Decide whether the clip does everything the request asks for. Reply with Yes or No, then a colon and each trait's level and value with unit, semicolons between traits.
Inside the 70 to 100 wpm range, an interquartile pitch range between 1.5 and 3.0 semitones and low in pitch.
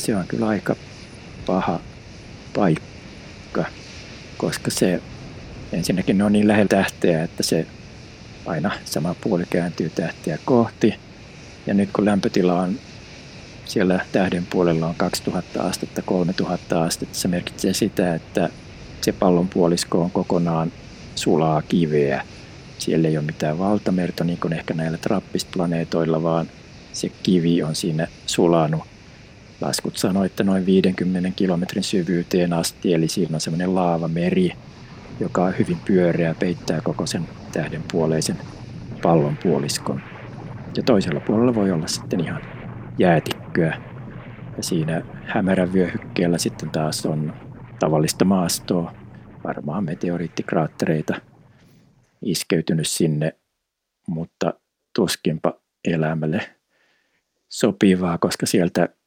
No: average, 115 wpm; narrow, 2.5 semitones; very low, 90 Hz